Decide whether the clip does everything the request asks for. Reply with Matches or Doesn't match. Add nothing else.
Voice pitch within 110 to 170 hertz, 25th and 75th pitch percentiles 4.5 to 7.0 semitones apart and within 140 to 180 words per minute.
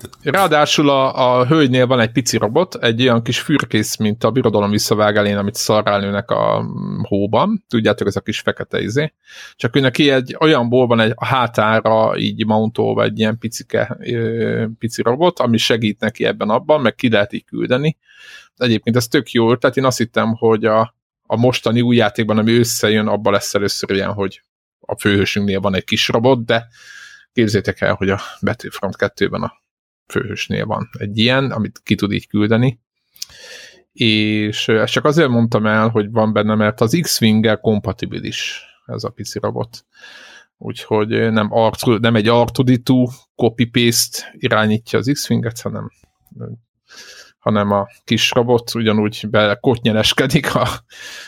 Doesn't match